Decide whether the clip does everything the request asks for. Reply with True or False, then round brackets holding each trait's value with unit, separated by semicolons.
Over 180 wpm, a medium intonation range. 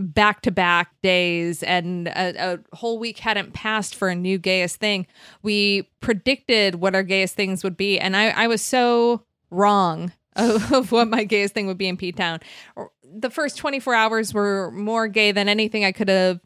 True (195 wpm; 3.1 semitones)